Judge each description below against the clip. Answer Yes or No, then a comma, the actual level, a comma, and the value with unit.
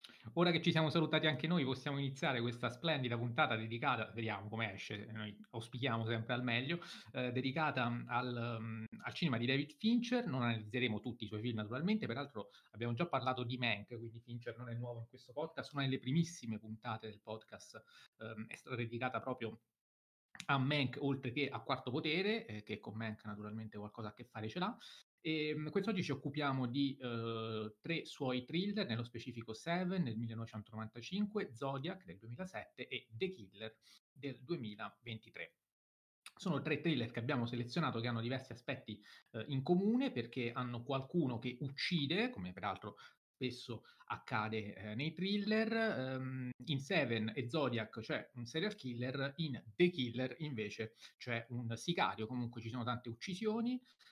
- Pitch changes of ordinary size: Yes, average, 4.9 semitones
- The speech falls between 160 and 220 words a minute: Yes, average, 165 wpm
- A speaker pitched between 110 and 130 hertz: Yes, low, 125 Hz